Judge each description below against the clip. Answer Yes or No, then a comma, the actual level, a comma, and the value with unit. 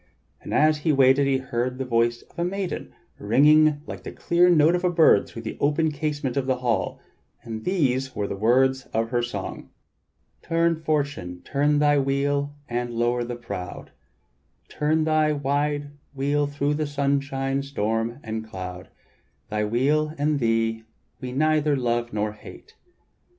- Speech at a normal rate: Yes, average, 155 wpm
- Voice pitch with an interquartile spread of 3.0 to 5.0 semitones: Yes, average, 4.0 semitones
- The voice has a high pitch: No, low, 135 Hz